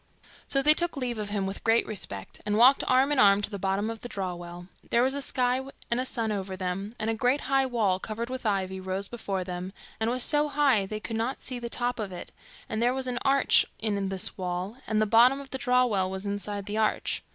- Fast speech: Yes, fast, 255 wpm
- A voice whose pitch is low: No, high, 220 Hz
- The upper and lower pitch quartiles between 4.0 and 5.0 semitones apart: Yes, average, 4.5 semitones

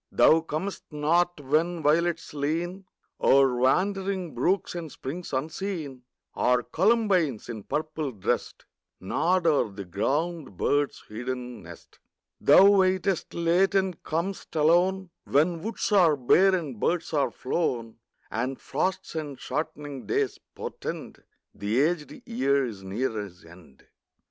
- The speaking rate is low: Yes, slow, 125 wpm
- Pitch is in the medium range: Yes, medium, 155 Hz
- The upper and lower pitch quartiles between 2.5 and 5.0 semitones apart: No, wide, 5.5 semitones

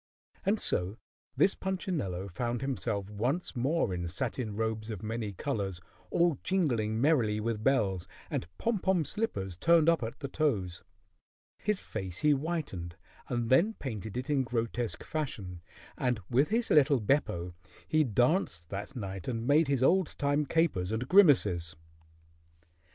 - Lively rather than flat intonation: Yes, wide, 7.0 semitones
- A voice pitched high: No, low, 120 Hz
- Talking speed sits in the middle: Yes, average, 145 wpm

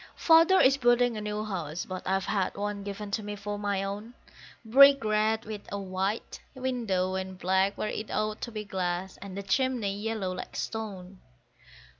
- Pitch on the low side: No, high, 205 Hz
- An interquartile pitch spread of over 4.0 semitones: No, narrow, 2.6 semitones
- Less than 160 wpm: No, average, 180 wpm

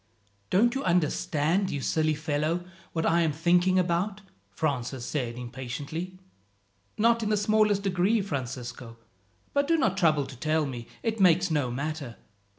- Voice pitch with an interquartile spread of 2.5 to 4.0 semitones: No, average, 5.3 semitones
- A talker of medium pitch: Yes, medium, 165 Hz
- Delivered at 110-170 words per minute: Yes, average, 150 wpm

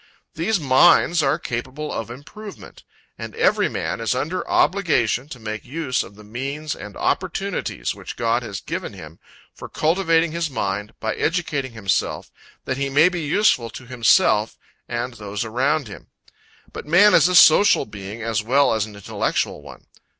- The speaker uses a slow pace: No, average, 165 wpm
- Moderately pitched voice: No, low, 130 Hz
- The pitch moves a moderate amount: No, wide, 6.2 semitones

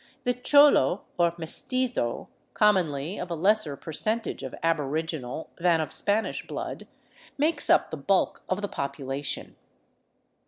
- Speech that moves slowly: Yes, slow, 125 wpm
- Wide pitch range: Yes, wide, 6.6 semitones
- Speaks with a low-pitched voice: No, medium, 170 Hz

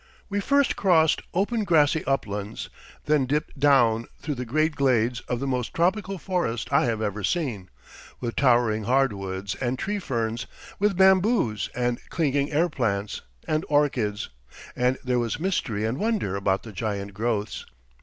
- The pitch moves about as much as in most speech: No, wide, 6.4 semitones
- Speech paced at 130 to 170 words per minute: Yes, average, 155 wpm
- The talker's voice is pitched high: No, low, 130 Hz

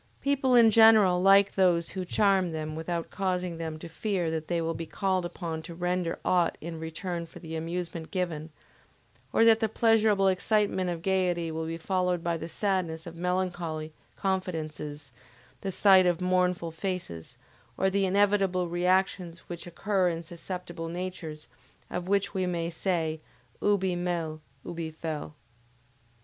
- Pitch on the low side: No, medium, 180 Hz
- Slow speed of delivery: No, average, 155 wpm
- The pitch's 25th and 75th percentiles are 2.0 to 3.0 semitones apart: Yes, narrow, 2.5 semitones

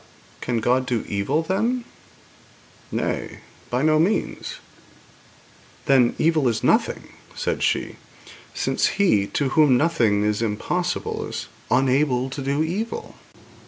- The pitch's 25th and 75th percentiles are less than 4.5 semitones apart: No, average, 5.2 semitones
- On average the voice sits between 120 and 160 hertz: Yes, low, 135 Hz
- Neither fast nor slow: No, slow, 125 wpm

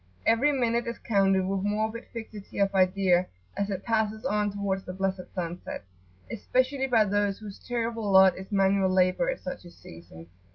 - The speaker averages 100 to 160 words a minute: No, average, 170 wpm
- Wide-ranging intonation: No, average, 3.0 semitones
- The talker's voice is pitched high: Yes, high, 200 Hz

